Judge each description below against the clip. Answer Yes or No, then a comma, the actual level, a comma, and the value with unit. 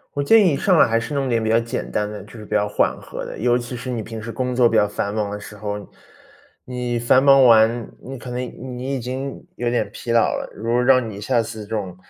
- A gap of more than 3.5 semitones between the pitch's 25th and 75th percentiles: No, average, 2.7 semitones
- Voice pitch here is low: Yes, low, 120 Hz